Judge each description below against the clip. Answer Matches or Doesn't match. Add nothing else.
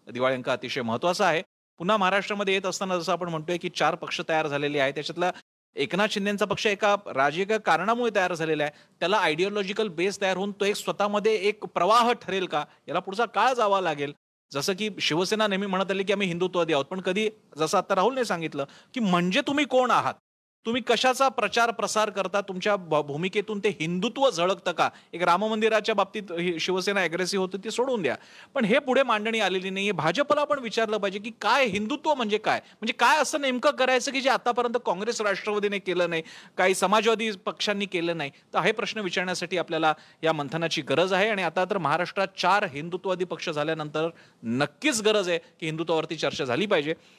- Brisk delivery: Matches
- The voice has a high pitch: Matches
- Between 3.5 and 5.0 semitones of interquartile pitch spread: Matches